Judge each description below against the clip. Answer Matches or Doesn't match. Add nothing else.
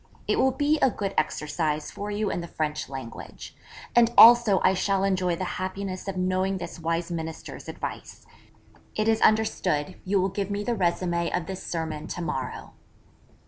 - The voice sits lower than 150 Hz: Doesn't match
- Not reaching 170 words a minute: Doesn't match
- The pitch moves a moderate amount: Matches